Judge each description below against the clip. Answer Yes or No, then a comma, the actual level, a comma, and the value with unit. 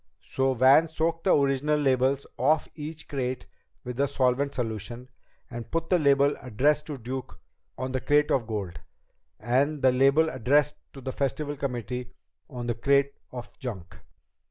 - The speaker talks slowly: No, average, 155 wpm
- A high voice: No, low, 135 Hz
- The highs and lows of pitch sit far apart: No, average, 2.8 semitones